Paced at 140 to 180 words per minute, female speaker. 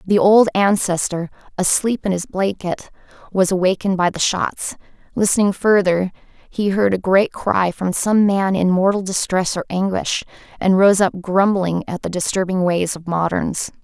Yes: average, 160 wpm; female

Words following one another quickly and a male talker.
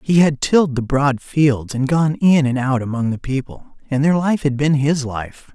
Yes: fast, 225 wpm; male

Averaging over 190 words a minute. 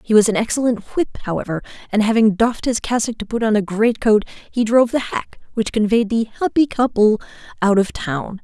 Yes: fast, 205 wpm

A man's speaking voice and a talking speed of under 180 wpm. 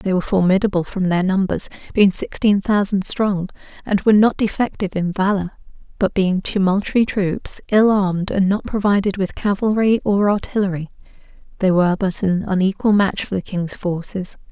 No: female; average, 160 wpm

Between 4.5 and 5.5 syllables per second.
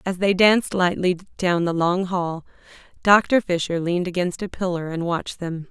Yes: 5.0 syllables/s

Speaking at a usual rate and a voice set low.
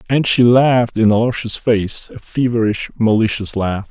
Yes: average, 155 wpm; low, 115 Hz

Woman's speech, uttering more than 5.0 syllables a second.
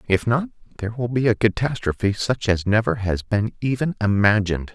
No: male; 5.6 syllables/s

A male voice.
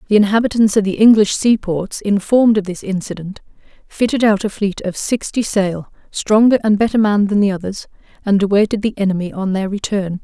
No: female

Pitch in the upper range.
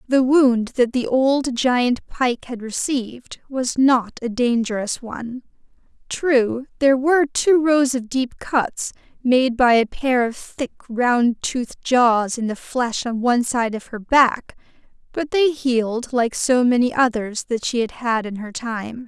Yes: high, 245 Hz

